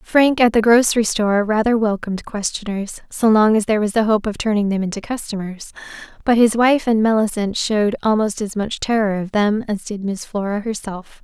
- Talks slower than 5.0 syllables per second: No, 5.4 syllables/s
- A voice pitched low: No, high, 215 Hz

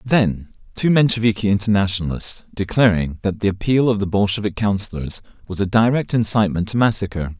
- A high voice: No, low, 100 Hz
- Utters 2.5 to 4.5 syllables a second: No, 5.9 syllables/s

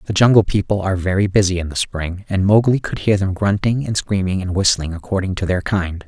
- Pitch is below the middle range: Yes, very low, 95 Hz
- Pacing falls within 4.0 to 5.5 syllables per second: No, 5.8 syllables/s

